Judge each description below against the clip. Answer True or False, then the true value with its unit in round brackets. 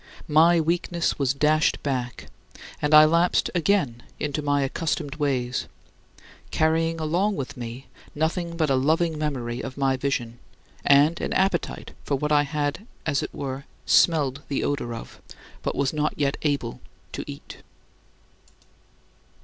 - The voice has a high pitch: False (145 Hz)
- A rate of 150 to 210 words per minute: False (140 wpm)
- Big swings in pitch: False (3.0 semitones)